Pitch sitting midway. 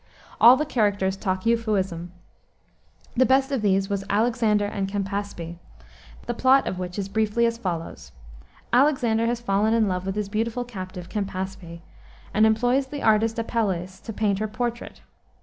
No: high, 210 Hz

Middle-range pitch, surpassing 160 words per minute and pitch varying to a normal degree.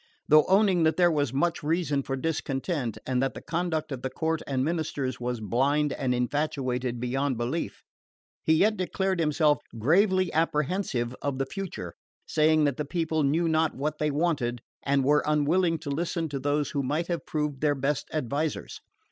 Yes: medium, 150 Hz; average, 175 wpm; average, 3.4 semitones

